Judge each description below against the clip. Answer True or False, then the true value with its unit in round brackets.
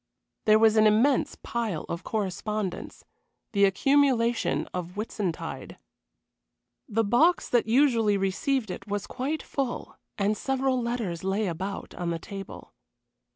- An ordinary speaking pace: False (125 wpm)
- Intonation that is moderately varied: True (3.8 semitones)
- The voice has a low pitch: False (215 Hz)